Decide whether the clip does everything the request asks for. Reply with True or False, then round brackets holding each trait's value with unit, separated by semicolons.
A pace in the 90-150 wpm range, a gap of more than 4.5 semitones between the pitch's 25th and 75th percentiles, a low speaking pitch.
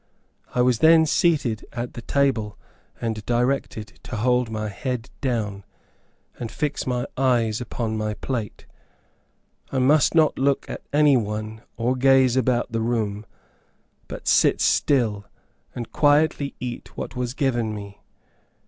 False (140 wpm; 3.4 semitones; 120 Hz)